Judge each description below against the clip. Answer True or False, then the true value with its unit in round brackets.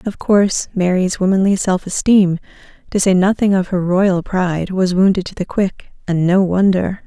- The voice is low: False (190 Hz)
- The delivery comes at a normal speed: True (180 wpm)